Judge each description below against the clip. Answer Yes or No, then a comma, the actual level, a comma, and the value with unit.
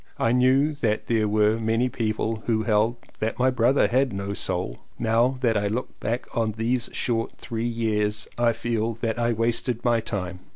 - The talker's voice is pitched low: Yes, low, 115 Hz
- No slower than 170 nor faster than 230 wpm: Yes, average, 180 wpm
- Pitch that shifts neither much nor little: No, narrow, 1.7 semitones